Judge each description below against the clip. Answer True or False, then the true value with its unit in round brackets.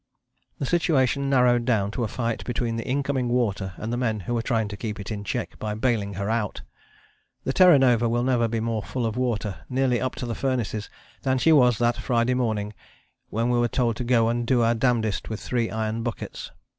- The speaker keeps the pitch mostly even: True (2.3 semitones)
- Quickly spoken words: True (220 wpm)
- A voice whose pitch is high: False (120 Hz)